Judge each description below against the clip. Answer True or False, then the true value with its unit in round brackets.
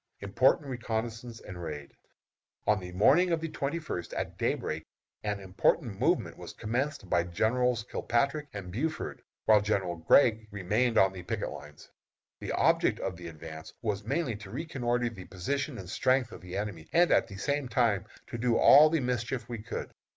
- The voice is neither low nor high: False (110 Hz)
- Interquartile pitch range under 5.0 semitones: False (5.3 semitones)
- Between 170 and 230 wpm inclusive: True (180 wpm)